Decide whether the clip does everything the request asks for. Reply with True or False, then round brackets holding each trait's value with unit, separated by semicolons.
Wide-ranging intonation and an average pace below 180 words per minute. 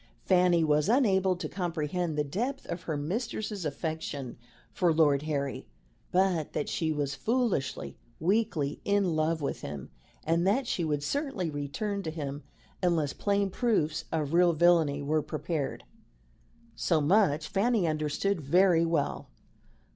False (4.5 semitones; 140 wpm)